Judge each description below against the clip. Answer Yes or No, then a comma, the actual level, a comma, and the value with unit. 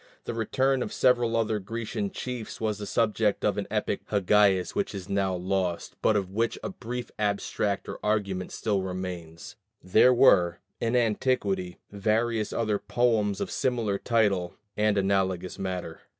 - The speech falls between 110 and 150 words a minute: No, average, 160 wpm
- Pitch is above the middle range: No, low, 105 Hz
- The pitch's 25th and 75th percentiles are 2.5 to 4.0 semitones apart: Yes, average, 3.2 semitones